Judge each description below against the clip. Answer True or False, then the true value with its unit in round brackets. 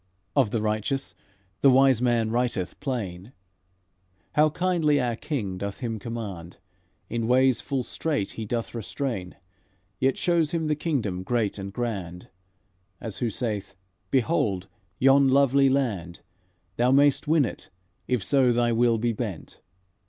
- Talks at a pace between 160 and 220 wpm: False (140 wpm)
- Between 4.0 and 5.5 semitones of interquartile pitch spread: True (4.6 semitones)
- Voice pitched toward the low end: True (120 Hz)